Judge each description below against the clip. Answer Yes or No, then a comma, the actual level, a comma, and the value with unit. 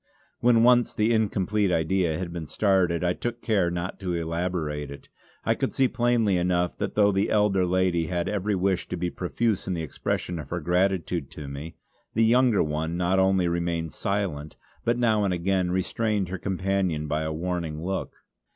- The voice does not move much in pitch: No, average, 3.1 semitones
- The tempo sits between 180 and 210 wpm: Yes, average, 185 wpm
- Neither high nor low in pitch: No, very low, 90 Hz